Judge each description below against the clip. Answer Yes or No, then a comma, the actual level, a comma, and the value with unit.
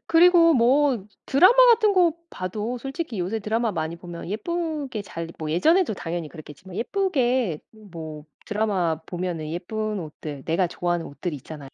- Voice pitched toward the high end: Yes, high, 200 Hz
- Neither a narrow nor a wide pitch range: No, wide, 8.4 semitones